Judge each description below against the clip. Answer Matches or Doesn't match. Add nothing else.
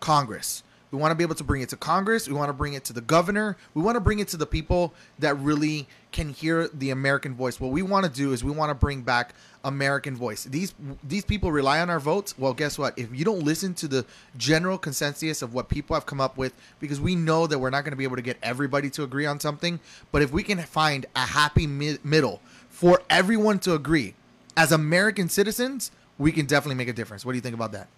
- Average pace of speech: Doesn't match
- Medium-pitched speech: Matches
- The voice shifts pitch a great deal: Doesn't match